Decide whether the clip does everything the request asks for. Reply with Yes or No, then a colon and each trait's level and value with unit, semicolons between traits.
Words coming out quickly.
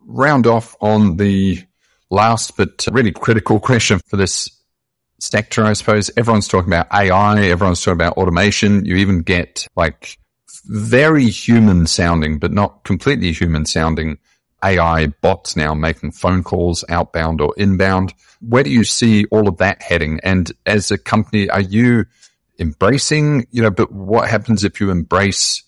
No: average, 155 wpm